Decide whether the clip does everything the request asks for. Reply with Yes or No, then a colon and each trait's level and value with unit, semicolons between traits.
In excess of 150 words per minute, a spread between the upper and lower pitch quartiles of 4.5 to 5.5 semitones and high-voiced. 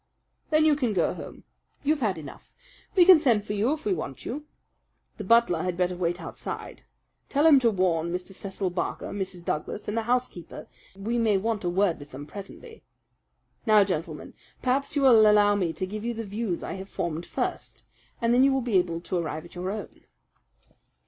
Yes: average, 200 wpm; average, 5.1 semitones; high, 205 Hz